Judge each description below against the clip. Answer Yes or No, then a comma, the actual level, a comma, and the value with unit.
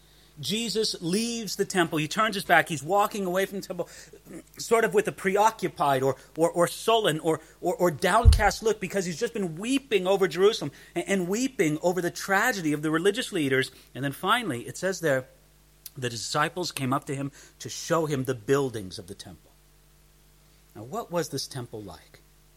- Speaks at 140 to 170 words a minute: No, average, 185 wpm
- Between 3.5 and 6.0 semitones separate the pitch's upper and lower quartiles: Yes, wide, 5.6 semitones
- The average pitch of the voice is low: No, medium, 165 Hz